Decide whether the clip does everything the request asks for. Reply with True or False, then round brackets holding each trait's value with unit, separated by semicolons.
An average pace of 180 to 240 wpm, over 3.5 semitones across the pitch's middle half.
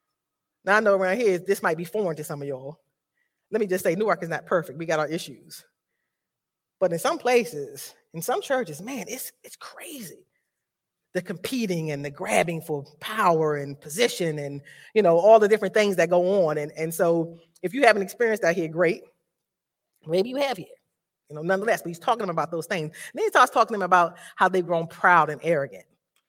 True (200 wpm; 5.1 semitones)